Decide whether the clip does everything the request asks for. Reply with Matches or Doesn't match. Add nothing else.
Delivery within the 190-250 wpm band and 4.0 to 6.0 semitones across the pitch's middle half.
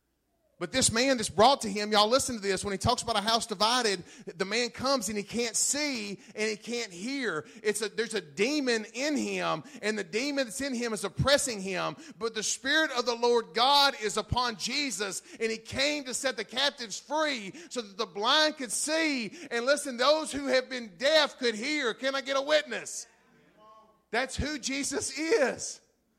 Matches